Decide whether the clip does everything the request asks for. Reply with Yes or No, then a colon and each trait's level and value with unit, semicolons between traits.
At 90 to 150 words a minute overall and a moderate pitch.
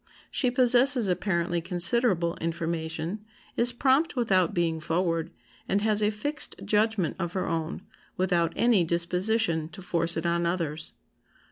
Yes: slow, 135 wpm; medium, 180 Hz